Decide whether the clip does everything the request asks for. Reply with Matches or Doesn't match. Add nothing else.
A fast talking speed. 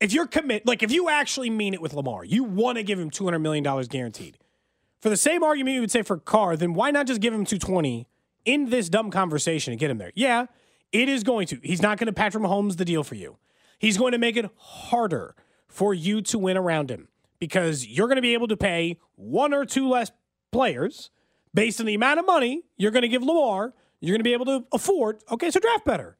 Matches